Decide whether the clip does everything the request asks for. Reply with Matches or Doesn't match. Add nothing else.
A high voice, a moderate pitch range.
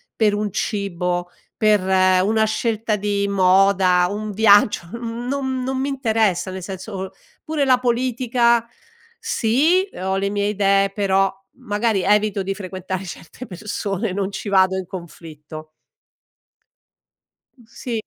Matches